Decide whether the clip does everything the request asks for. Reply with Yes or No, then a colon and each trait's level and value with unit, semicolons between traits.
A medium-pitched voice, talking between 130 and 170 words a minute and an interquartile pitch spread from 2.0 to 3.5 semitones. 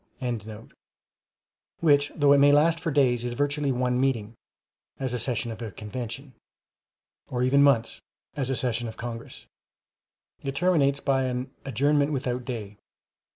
No: low, 130 Hz; average, 150 wpm; average, 2.8 semitones